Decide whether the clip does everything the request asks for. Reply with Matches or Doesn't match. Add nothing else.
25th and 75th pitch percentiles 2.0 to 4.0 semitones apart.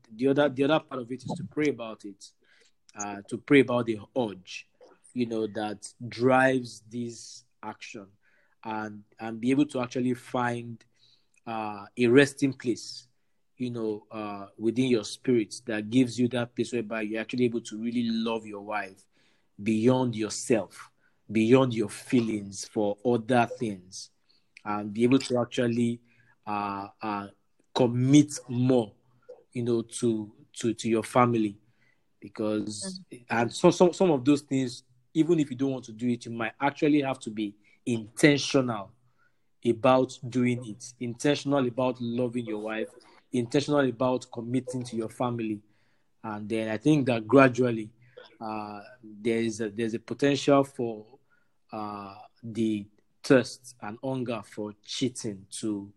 Matches